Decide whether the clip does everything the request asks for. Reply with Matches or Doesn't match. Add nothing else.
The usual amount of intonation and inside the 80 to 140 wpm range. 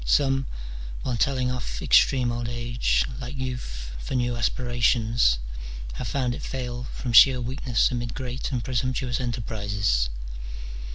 Doesn't match